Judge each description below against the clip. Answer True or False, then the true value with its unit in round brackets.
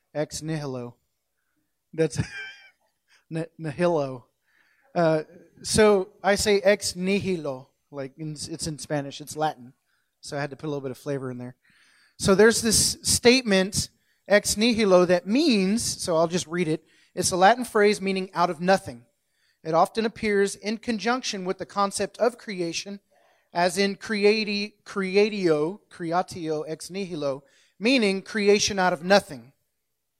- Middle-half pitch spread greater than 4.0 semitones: True (5.1 semitones)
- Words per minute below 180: True (145 wpm)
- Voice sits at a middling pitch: True (180 Hz)